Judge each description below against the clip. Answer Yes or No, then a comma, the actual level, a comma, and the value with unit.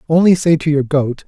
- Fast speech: Yes, fast, 235 wpm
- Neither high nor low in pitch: Yes, medium, 155 Hz